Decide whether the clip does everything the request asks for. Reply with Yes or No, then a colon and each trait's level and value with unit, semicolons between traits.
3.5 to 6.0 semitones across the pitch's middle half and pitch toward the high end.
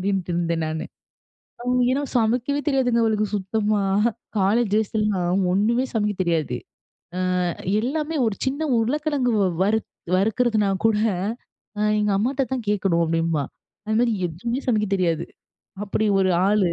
Yes: average, 4.2 semitones; high, 215 Hz